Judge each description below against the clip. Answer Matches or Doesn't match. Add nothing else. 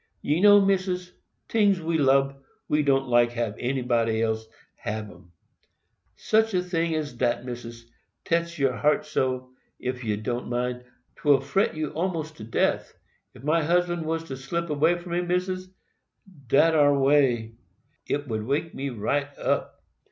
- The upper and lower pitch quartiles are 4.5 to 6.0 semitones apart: Matches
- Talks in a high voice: Doesn't match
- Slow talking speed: Doesn't match